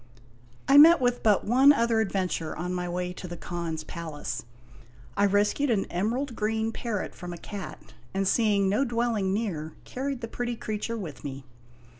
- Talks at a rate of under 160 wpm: No, average, 170 wpm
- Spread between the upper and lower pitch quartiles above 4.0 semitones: Yes, average, 4.8 semitones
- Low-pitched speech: No, high, 205 Hz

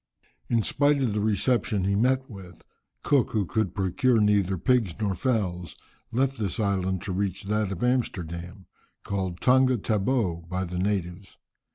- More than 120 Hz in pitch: No, low, 100 Hz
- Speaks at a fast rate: No, average, 155 wpm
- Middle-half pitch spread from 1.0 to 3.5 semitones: No, average, 4.5 semitones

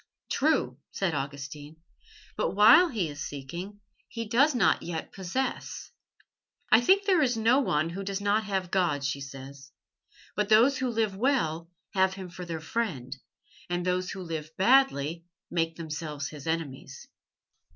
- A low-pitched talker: No, medium, 180 Hz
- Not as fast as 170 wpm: Yes, average, 150 wpm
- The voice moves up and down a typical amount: No, wide, 6.2 semitones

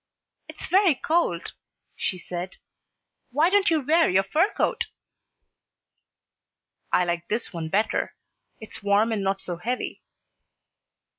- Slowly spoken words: Yes, slow, 125 wpm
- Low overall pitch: No, high, 215 Hz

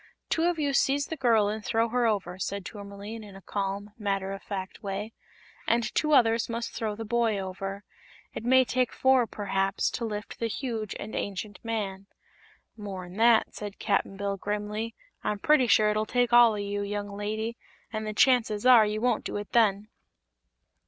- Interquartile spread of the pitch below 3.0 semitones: Yes, narrow, 2.6 semitones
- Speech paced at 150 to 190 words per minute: Yes, average, 185 wpm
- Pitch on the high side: Yes, high, 215 Hz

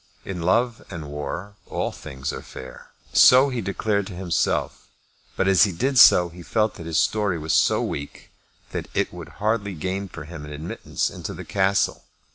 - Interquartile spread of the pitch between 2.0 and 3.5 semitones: No, average, 3.9 semitones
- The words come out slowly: No, average, 185 wpm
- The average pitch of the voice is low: Yes, very low, 95 Hz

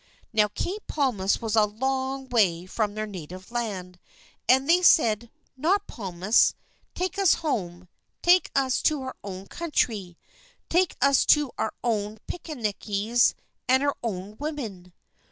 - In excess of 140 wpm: No, slow, 135 wpm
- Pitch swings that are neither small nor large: No, wide, 5.7 semitones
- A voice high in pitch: Yes, high, 230 Hz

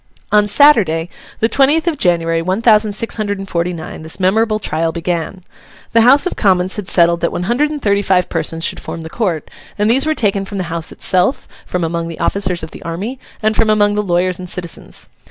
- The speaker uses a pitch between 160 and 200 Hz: Yes, high, 190 Hz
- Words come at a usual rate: No, fast, 220 wpm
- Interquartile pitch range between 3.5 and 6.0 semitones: Yes, average, 4.2 semitones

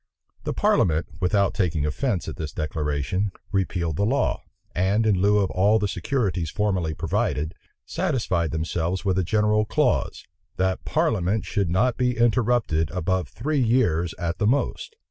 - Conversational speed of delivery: Yes, average, 150 wpm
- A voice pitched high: No, very low, 95 Hz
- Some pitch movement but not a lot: Yes, average, 4.4 semitones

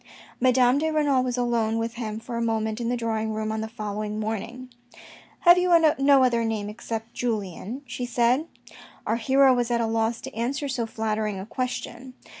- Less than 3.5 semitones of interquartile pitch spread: Yes, narrow, 2.5 semitones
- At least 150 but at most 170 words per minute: No, average, 195 wpm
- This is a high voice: Yes, high, 235 Hz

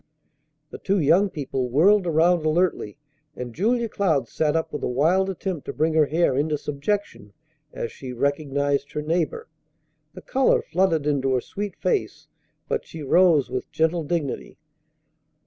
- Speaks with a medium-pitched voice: Yes, medium, 160 Hz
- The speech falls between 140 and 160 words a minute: Yes, average, 155 wpm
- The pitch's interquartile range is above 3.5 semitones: Yes, average, 4.4 semitones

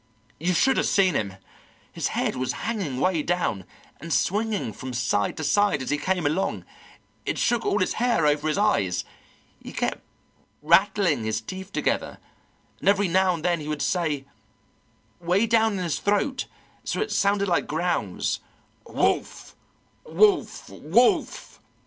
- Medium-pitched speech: Yes, medium, 180 Hz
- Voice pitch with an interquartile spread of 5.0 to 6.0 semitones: Yes, wide, 5.5 semitones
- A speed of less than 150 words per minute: No, average, 155 wpm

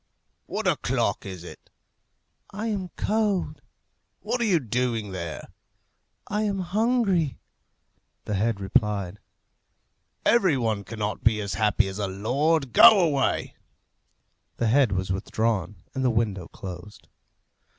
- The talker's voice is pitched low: Yes, low, 115 Hz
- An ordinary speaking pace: No, slow, 125 wpm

